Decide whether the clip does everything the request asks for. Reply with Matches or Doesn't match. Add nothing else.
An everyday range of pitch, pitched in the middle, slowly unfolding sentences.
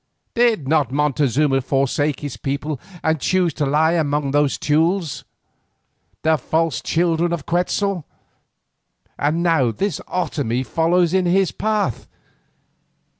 Matches